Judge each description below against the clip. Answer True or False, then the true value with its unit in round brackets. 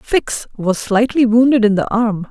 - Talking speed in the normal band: True (180 wpm)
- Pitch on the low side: False (225 Hz)